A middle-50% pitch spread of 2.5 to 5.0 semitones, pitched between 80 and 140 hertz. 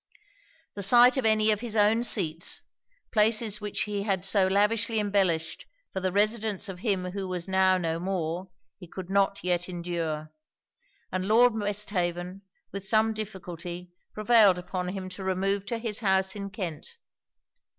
No: average, 2.8 semitones; high, 195 Hz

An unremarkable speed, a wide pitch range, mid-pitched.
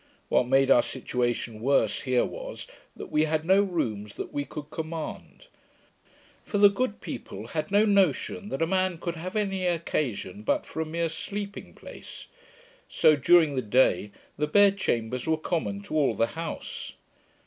Yes: average, 170 wpm; wide, 6.7 semitones; medium, 160 Hz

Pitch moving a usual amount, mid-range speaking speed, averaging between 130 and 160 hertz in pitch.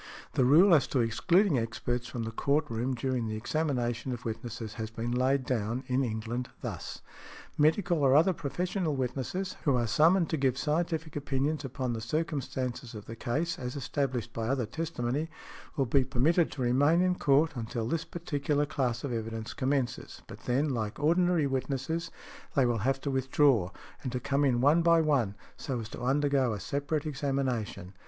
Yes: average, 3.9 semitones; average, 175 wpm; low, 135 Hz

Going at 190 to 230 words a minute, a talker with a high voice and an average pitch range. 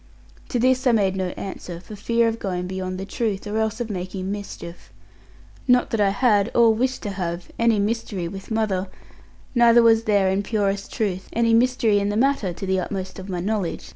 Yes: average, 200 wpm; high, 205 Hz; average, 3.3 semitones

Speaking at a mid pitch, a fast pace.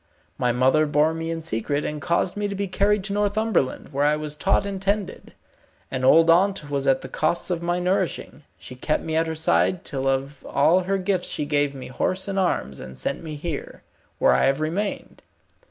Yes: medium, 160 Hz; fast, 210 wpm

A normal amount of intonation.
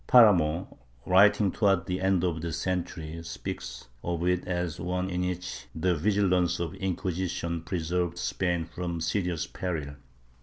No: narrow, 1.7 semitones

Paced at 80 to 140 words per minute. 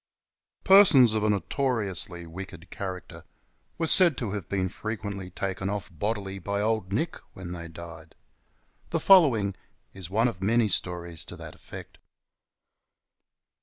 Yes: slow, 135 wpm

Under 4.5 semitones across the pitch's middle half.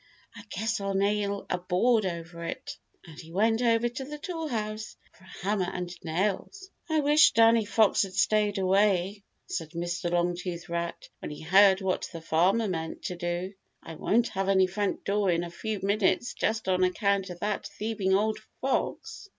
Yes: average, 3.5 semitones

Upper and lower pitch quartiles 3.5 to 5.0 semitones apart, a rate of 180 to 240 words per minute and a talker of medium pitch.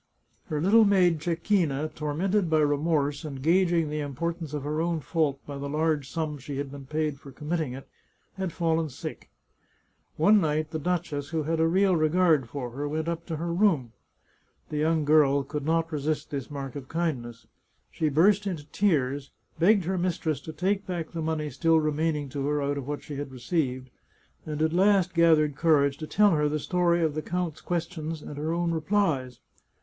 No: average, 2.8 semitones; average, 195 wpm; medium, 155 Hz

